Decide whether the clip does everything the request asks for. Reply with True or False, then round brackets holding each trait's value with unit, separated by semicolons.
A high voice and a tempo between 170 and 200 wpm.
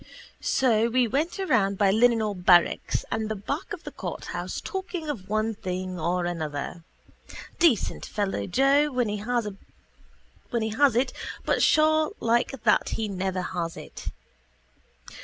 False (215 Hz; 140 wpm)